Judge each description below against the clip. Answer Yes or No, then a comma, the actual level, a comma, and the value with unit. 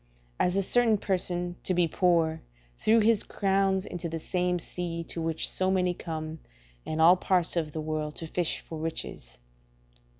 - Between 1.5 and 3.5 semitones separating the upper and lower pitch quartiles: Yes, narrow, 2.6 semitones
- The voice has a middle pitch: Yes, medium, 175 Hz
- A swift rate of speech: No, average, 165 wpm